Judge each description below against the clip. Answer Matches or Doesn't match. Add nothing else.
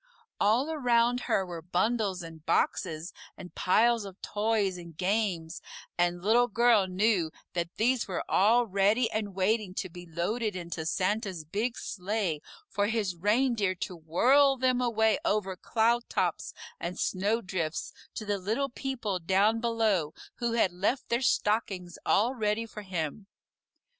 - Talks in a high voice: Matches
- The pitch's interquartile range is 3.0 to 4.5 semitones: Matches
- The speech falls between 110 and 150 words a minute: Matches